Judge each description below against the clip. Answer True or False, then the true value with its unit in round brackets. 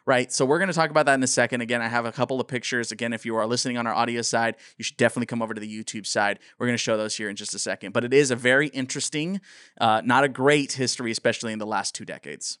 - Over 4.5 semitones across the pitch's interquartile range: False (2.7 semitones)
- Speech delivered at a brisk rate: True (290 wpm)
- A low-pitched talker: True (120 Hz)